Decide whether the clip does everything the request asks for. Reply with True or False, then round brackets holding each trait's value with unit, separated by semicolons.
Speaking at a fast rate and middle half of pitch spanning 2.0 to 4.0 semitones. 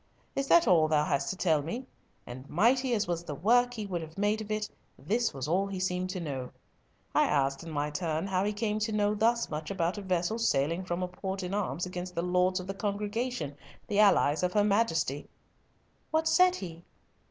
False (215 wpm; 4.4 semitones)